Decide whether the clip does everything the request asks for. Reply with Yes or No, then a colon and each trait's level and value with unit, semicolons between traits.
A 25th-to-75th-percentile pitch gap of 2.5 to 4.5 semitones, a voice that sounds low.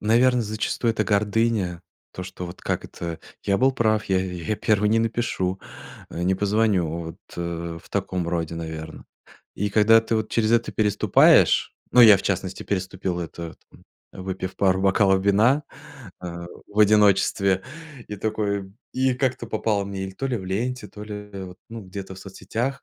Yes: average, 3.2 semitones; low, 100 Hz